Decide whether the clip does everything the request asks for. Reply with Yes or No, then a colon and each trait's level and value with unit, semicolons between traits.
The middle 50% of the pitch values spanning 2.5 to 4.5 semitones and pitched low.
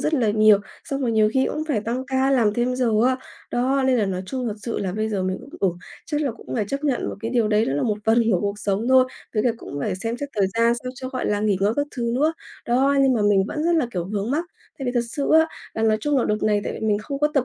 No: average, 4.0 semitones; high, 235 Hz